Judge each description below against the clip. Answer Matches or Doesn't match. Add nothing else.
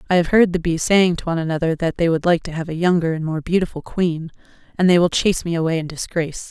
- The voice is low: Doesn't match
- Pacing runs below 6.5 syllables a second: Doesn't match